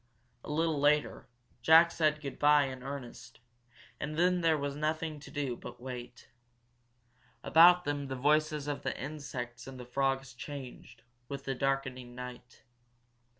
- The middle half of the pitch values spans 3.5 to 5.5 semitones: No, average, 2.9 semitones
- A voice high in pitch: No, medium, 140 Hz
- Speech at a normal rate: Yes, average, 145 wpm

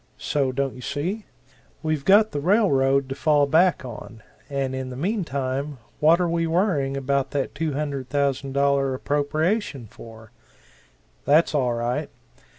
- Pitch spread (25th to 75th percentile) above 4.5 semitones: No, average, 3.2 semitones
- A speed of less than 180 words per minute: Yes, average, 140 wpm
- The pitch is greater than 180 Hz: No, medium, 140 Hz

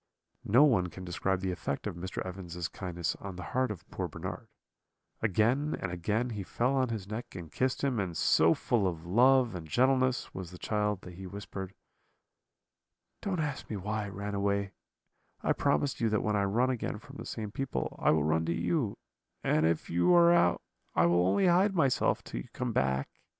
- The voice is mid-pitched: No, low, 100 Hz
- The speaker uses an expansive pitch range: Yes, wide, 6.0 semitones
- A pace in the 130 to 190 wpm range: No, average, 200 wpm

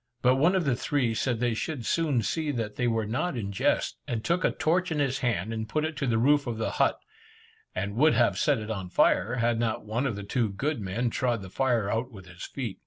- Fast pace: Yes, fast, 250 wpm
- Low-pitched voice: Yes, low, 120 Hz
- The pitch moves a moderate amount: Yes, average, 4.1 semitones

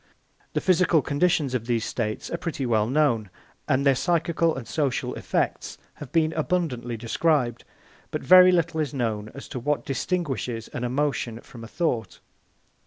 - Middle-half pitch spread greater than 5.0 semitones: Yes, wide, 5.5 semitones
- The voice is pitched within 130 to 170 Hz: Yes, medium, 140 Hz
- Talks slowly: No, average, 160 wpm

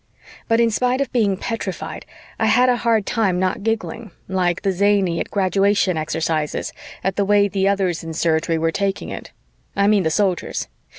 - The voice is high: Yes, high, 195 Hz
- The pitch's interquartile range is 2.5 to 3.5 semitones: Yes, average, 3.2 semitones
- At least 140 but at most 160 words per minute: No, average, 185 wpm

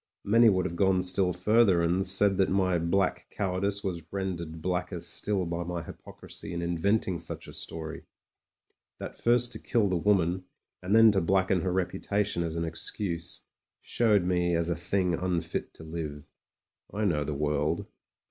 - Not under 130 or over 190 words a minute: Yes, average, 170 wpm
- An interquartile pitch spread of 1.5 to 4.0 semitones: Yes, narrow, 2.6 semitones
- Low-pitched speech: Yes, very low, 90 Hz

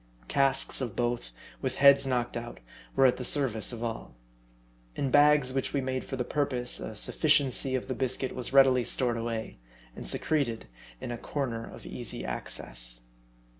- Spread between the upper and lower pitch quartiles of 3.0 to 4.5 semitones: No, narrow, 2.5 semitones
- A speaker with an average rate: Yes, average, 170 wpm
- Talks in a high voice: No, low, 125 Hz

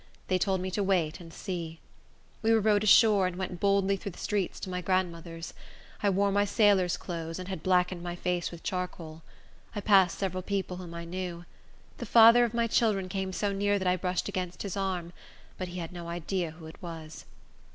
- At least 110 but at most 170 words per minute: No, fast, 205 wpm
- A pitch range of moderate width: No, narrow, 2.3 semitones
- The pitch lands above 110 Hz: Yes, medium, 185 Hz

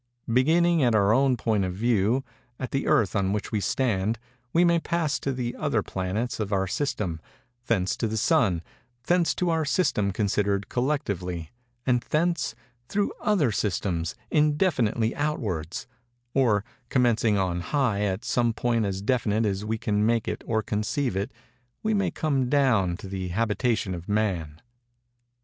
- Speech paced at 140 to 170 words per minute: Yes, average, 145 wpm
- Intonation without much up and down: No, average, 5.1 semitones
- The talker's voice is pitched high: No, low, 115 Hz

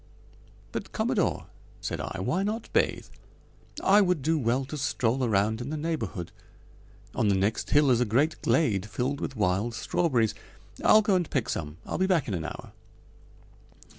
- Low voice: Yes, low, 125 Hz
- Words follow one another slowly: No, average, 170 wpm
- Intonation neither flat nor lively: No, wide, 6.9 semitones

